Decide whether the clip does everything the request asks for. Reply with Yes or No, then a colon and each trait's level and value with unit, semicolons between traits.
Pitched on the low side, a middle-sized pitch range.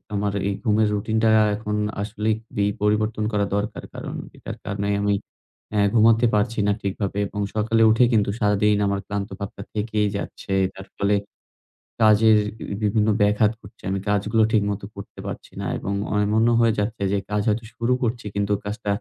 No: low, 105 Hz; narrow, 1.3 semitones